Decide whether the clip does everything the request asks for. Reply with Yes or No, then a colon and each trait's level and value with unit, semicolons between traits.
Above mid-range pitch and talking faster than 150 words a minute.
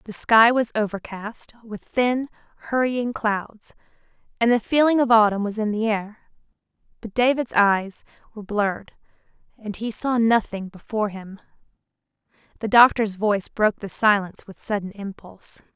No: high, 215 Hz; average, 140 wpm